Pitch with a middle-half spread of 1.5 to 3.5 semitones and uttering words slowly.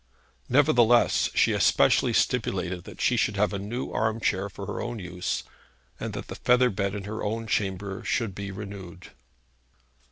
No: average, 2.8 semitones; average, 165 wpm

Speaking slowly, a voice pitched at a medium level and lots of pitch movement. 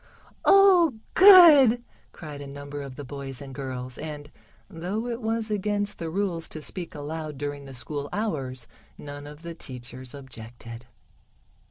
No: average, 150 wpm; medium, 150 Hz; wide, 7.0 semitones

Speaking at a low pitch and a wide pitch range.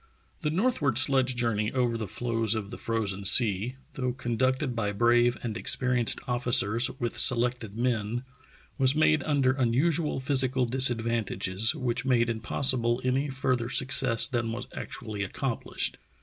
No: low, 120 Hz; narrow, 2.4 semitones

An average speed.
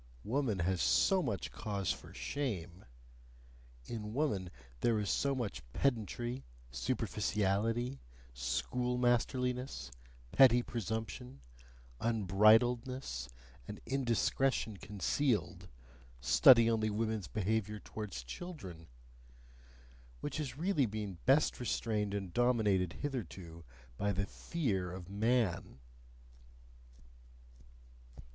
No: slow, 90 wpm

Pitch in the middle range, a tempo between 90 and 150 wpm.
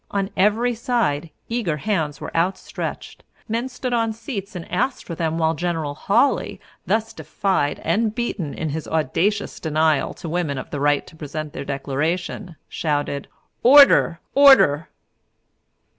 Yes: medium, 170 Hz; average, 145 wpm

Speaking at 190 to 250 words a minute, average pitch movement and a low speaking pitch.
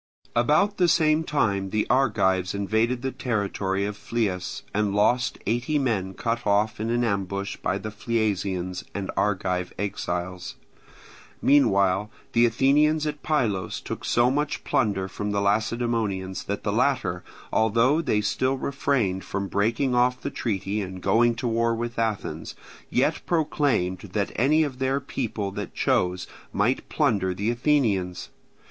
No: average, 145 wpm; average, 4.5 semitones; low, 110 Hz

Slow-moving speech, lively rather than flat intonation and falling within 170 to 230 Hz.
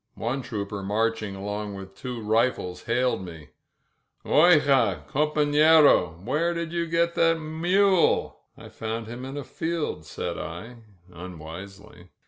No: slow, 125 wpm; wide, 7.8 semitones; low, 120 Hz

